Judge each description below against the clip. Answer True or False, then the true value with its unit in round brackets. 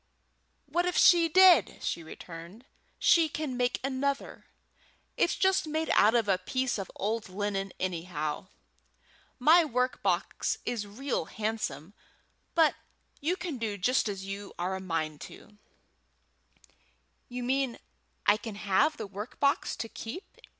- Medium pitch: False (225 Hz)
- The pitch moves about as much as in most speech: False (6.4 semitones)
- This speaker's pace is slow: False (145 wpm)